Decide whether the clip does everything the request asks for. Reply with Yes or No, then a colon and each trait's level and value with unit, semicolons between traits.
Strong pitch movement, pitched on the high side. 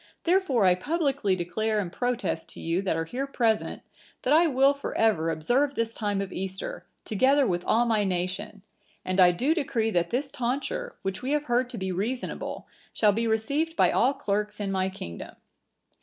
Yes: wide, 6.0 semitones; high, 220 Hz